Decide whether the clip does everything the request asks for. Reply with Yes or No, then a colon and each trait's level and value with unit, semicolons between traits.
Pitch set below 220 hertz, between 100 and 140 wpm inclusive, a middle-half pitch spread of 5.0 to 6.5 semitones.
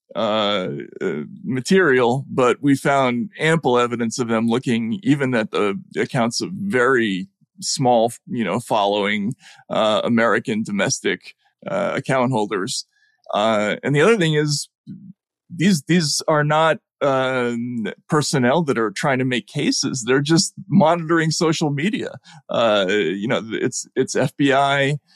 Yes: medium, 140 Hz; slow, 135 wpm; wide, 5.6 semitones